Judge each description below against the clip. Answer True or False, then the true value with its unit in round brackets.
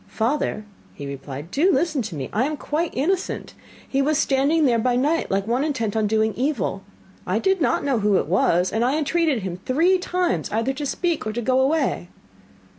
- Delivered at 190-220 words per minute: True (200 wpm)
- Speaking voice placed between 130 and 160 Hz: False (260 Hz)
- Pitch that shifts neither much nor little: False (6.1 semitones)